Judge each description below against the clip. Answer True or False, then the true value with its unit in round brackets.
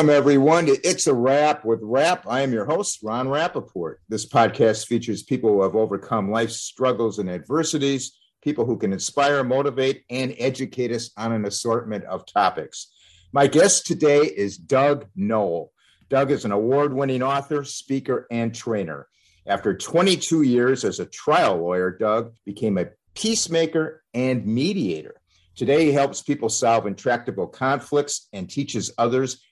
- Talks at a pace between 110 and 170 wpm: True (150 wpm)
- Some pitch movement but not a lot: True (4.3 semitones)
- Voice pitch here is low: True (125 Hz)